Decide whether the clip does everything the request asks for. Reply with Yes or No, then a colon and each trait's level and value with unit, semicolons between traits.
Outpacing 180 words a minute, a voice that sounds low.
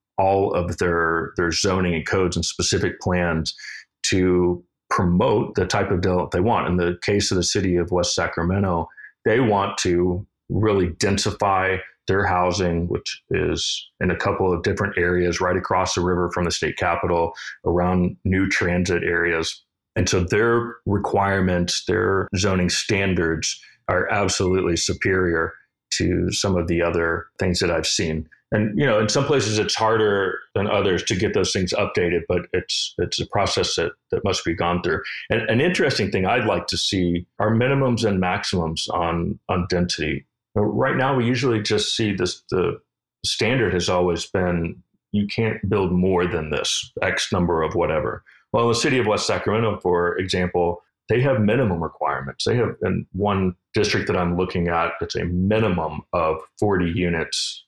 No: average, 170 wpm; very low, 90 Hz